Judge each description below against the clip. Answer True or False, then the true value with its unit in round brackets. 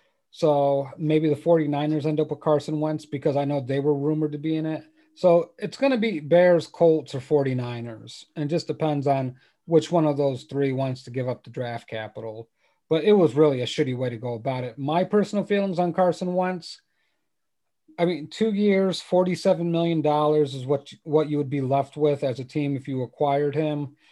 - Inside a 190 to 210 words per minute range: True (205 wpm)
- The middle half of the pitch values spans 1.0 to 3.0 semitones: False (3.5 semitones)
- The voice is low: False (150 Hz)